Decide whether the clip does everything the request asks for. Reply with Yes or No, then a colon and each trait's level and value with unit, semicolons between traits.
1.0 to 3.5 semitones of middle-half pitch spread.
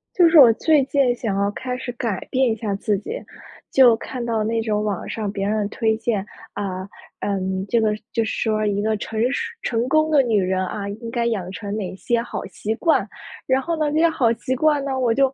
No: average, 3.9 semitones